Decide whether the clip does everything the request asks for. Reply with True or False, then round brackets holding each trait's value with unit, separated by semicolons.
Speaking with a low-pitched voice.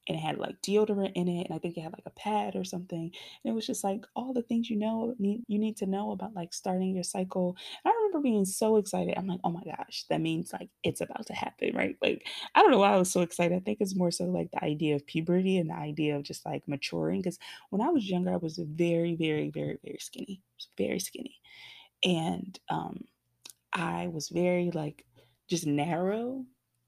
False (180 Hz)